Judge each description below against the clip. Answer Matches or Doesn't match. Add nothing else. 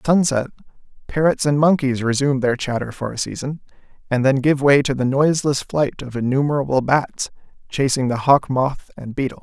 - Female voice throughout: Doesn't match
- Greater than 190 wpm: Doesn't match